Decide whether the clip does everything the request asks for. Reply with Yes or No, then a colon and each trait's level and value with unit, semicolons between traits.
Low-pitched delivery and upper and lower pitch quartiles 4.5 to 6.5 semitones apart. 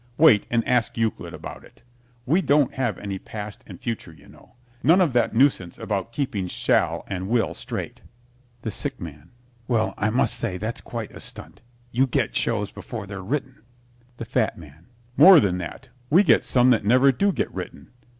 Yes: low, 115 Hz; average, 4.8 semitones